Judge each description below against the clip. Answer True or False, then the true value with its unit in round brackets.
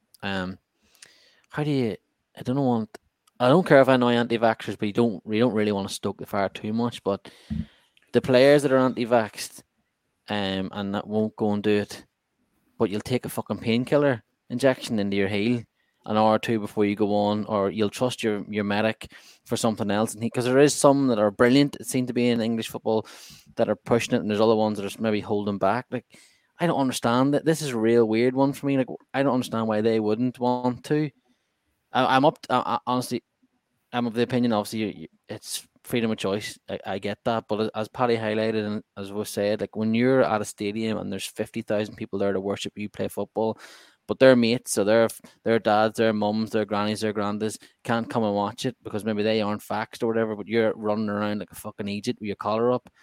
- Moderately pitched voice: False (110 Hz)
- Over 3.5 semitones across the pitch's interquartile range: False (2.8 semitones)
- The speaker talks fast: True (225 wpm)